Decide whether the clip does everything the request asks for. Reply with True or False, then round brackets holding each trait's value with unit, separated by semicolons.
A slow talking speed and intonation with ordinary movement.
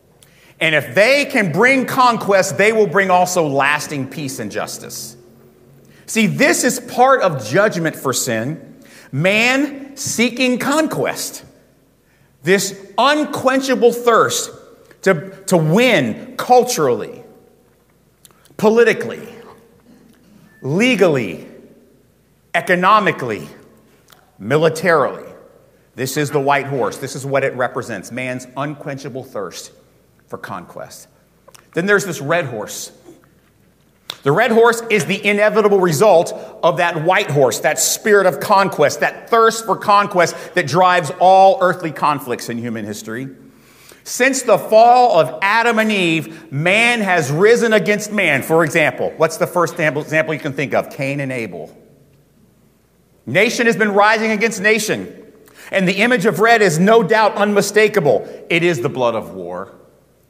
False (130 wpm; 6.6 semitones)